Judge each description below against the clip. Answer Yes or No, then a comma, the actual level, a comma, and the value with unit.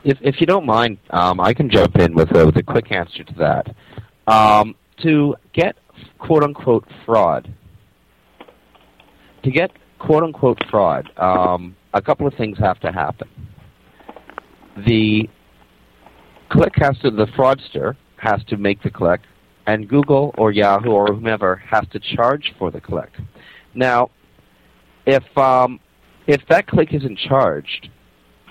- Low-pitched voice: Yes, low, 110 Hz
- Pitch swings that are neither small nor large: No, wide, 6.5 semitones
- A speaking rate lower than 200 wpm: Yes, average, 145 wpm